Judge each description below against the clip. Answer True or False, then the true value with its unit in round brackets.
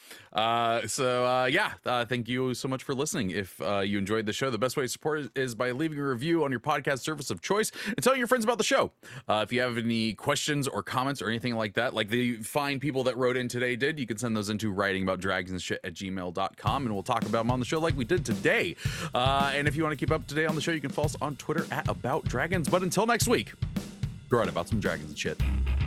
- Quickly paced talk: True (275 wpm)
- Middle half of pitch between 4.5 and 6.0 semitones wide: True (5.0 semitones)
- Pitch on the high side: False (125 Hz)